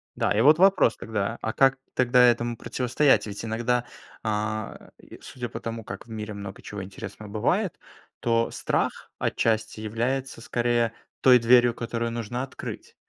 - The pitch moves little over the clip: Yes, narrow, 2.2 semitones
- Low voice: Yes, low, 115 Hz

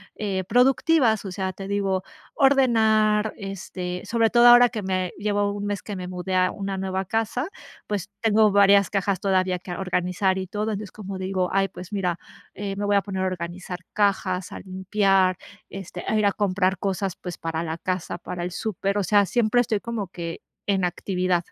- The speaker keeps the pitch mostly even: Yes, narrow, 2.2 semitones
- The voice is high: Yes, high, 195 Hz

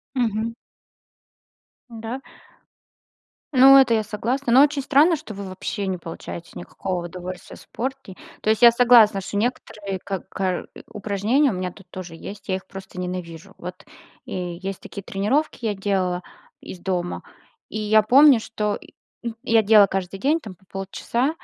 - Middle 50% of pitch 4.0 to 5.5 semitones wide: Yes, average, 4.3 semitones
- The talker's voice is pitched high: Yes, high, 205 Hz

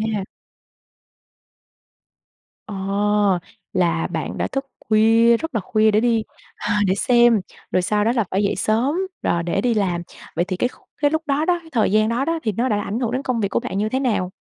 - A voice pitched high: Yes, high, 220 Hz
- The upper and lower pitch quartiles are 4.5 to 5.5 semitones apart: No, average, 3.7 semitones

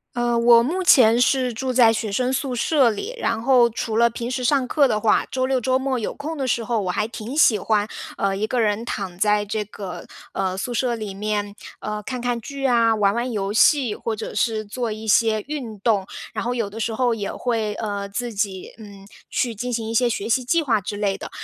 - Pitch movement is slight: No, average, 3.0 semitones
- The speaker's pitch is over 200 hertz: Yes, high, 230 Hz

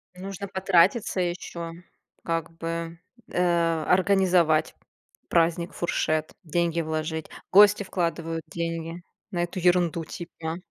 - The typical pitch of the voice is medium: Yes, medium, 170 Hz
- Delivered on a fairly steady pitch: Yes, narrow, 1.5 semitones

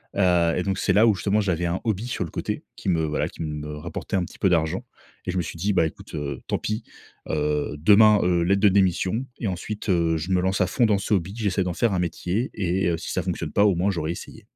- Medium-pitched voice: No, very low, 90 Hz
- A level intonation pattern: No, average, 3.3 semitones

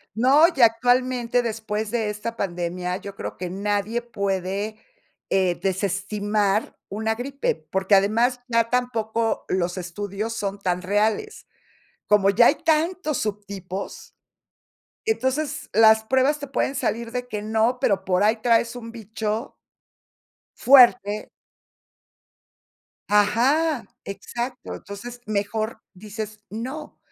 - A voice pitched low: No, high, 220 Hz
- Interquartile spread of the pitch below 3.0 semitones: No, average, 3.5 semitones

